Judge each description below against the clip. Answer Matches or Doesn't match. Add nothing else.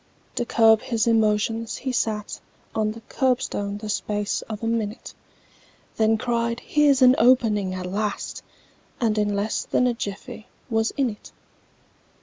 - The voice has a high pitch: Matches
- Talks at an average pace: Matches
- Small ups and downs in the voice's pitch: Matches